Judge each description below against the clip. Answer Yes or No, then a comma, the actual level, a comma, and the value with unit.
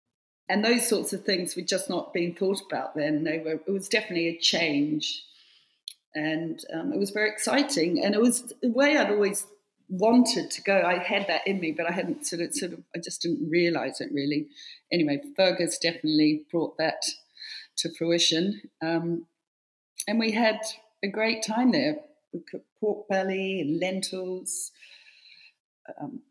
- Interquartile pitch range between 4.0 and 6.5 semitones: Yes, average, 4.8 semitones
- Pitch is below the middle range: No, high, 190 Hz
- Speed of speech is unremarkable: Yes, average, 170 wpm